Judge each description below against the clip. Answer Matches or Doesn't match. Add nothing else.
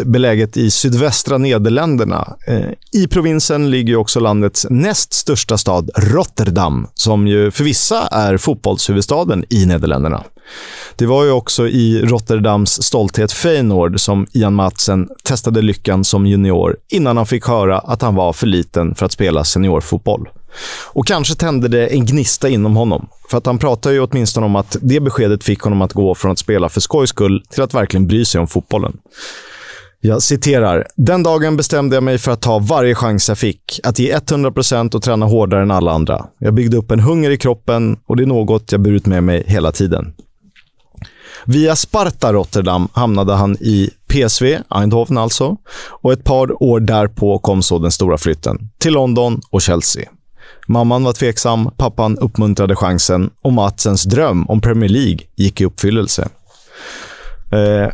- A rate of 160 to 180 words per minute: Matches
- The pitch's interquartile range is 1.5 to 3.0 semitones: Doesn't match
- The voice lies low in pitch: Matches